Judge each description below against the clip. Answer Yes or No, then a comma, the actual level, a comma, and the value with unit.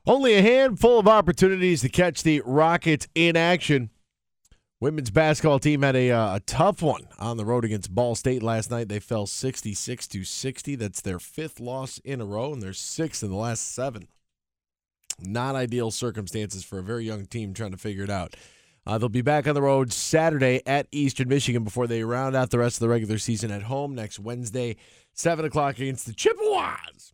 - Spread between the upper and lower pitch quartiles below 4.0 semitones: No, average, 5.1 semitones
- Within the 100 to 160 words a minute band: No, average, 200 wpm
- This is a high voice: No, low, 125 Hz